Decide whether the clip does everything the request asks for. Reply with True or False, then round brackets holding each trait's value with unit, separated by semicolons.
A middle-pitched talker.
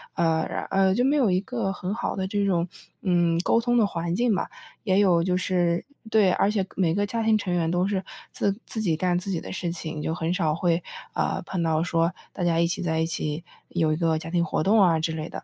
True (180 Hz)